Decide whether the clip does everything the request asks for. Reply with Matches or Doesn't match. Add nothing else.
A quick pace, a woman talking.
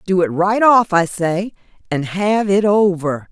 Doesn't match